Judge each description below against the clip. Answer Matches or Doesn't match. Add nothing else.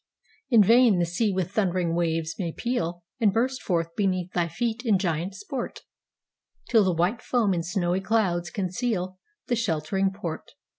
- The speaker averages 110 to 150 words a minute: Matches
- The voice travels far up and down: Doesn't match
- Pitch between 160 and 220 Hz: Matches